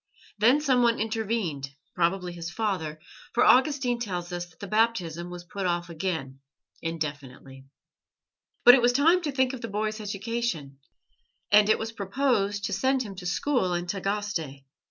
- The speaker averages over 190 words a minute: No, average, 155 wpm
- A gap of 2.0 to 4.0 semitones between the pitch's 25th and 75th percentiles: No, average, 5.3 semitones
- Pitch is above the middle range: Yes, high, 200 Hz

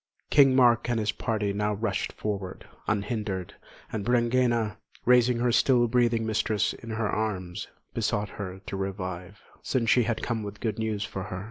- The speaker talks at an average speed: Yes, average, 165 wpm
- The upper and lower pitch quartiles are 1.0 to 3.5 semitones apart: Yes, average, 2.7 semitones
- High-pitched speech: No, low, 110 Hz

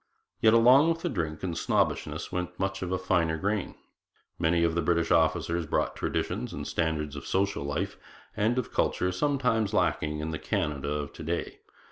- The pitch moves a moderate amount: Yes, average, 4.3 semitones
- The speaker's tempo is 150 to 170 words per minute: No, average, 180 wpm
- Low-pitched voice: Yes, very low, 85 Hz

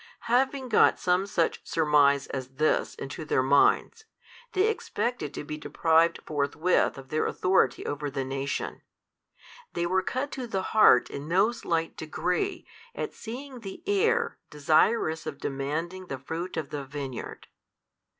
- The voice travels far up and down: Yes, wide, 6.9 semitones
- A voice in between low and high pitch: Yes, medium, 165 Hz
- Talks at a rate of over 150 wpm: No, average, 145 wpm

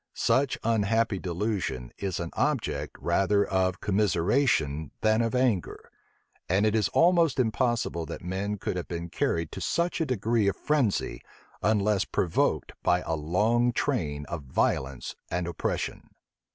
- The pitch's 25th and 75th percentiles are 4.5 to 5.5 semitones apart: Yes, average, 5.2 semitones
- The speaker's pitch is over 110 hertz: No, low, 100 Hz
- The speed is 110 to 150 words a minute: Yes, average, 140 wpm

